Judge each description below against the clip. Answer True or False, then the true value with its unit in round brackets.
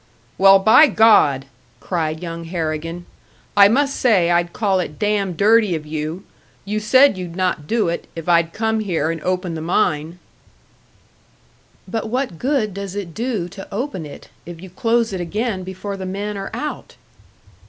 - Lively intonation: False (4.2 semitones)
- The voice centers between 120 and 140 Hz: False (190 Hz)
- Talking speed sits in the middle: True (165 wpm)